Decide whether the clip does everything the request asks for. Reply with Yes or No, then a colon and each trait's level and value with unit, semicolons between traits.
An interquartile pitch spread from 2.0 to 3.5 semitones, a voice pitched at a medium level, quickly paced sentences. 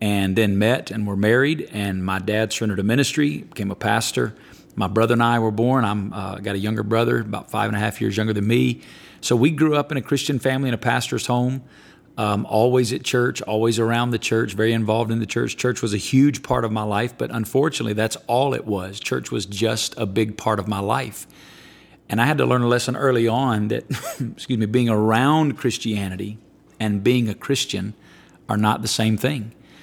No: average, 3.0 semitones; low, 115 Hz; fast, 215 wpm